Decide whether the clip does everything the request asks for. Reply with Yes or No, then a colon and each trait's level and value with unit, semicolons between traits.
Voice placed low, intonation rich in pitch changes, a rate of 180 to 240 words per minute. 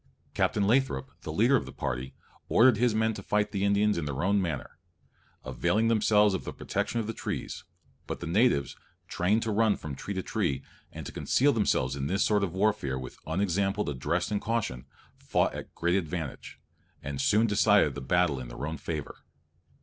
Yes: low, 100 Hz; wide, 6.4 semitones; average, 190 wpm